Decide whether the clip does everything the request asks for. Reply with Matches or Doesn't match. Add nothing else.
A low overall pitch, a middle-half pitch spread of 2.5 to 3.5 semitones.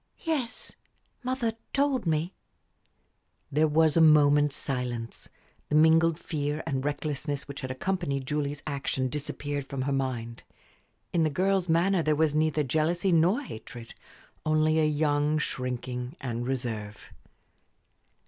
Doesn't match